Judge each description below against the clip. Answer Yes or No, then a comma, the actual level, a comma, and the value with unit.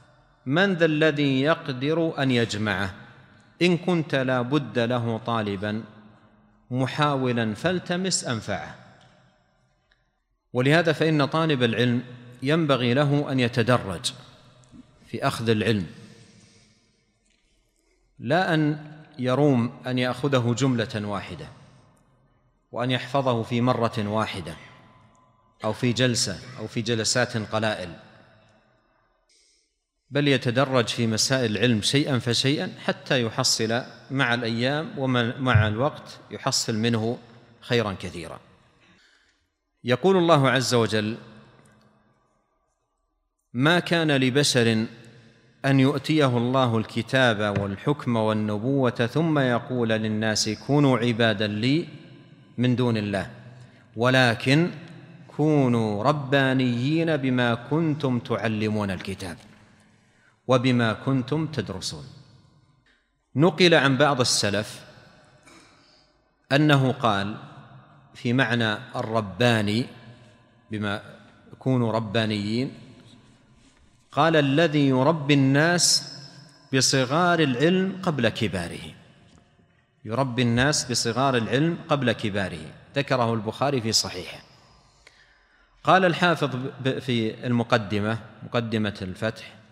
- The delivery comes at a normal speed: Yes, average, 85 wpm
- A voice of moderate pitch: No, low, 125 Hz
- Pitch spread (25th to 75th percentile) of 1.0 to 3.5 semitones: No, average, 3.9 semitones